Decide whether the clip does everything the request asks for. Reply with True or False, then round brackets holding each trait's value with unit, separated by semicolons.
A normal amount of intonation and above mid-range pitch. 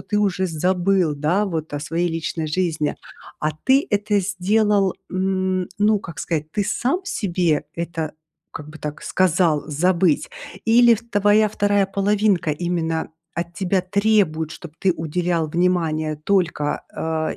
False (3.9 semitones; 180 Hz)